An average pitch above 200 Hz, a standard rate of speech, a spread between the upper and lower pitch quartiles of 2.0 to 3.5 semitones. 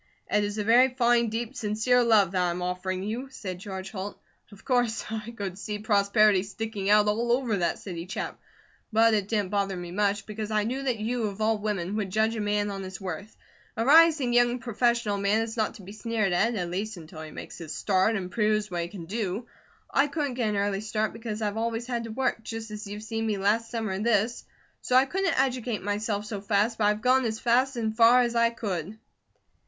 No: high, 215 Hz; fast, 225 wpm; average, 2.7 semitones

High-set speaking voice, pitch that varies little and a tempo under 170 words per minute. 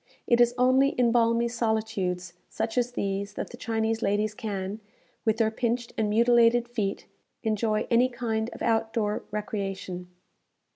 Yes: high, 225 Hz; narrow, 2.2 semitones; average, 150 wpm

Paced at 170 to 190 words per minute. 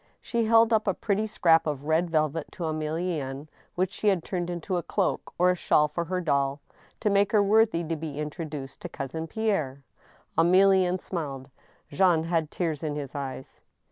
Yes: average, 180 wpm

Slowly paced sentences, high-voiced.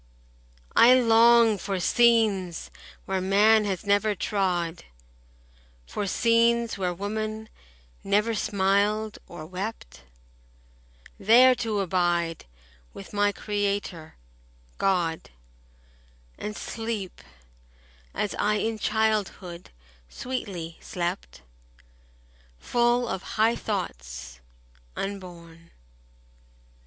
Yes: slow, 85 wpm; high, 205 Hz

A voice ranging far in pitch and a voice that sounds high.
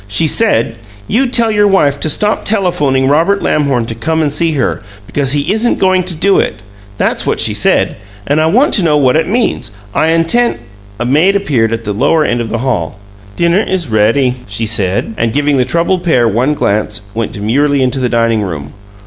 No: wide, 6.9 semitones; medium, 140 Hz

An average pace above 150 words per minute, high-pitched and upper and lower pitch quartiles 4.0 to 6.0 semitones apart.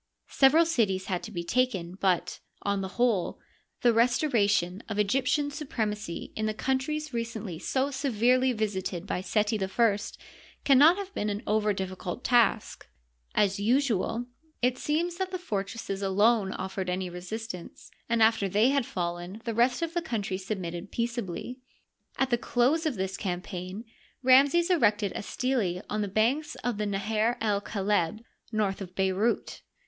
Yes: average, 160 wpm; high, 215 Hz; average, 4.8 semitones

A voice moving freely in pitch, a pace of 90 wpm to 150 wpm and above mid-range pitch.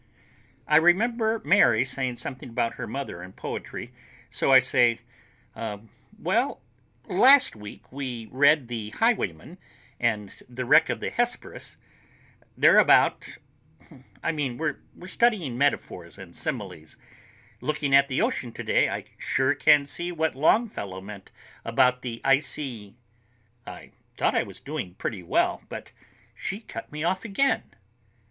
No: wide, 5.8 semitones; slow, 135 wpm; low, 135 Hz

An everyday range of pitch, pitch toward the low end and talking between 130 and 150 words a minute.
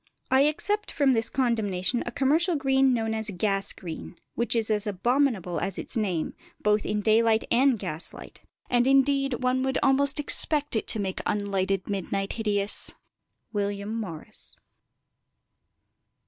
No: average, 4.9 semitones; high, 225 Hz; average, 140 wpm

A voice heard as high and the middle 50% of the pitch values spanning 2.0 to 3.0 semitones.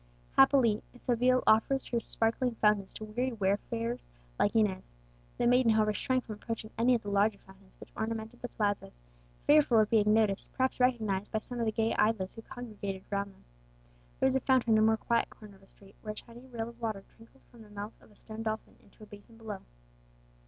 Yes: high, 220 Hz; narrow, 2.4 semitones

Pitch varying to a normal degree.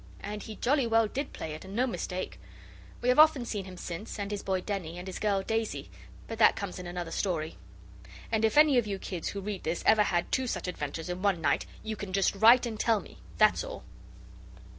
Yes: average, 3.8 semitones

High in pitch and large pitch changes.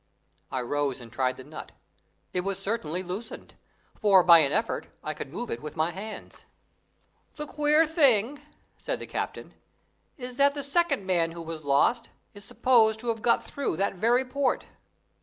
Yes: high, 205 Hz; wide, 7.5 semitones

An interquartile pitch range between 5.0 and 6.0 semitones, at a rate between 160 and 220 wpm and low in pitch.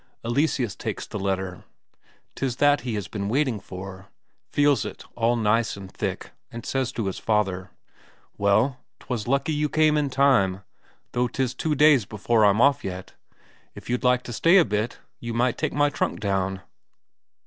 Yes: wide, 5.4 semitones; average, 170 wpm; low, 120 Hz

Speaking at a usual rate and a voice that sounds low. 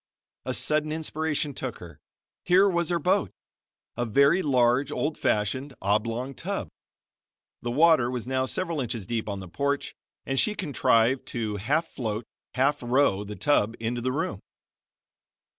Yes: average, 150 wpm; low, 130 Hz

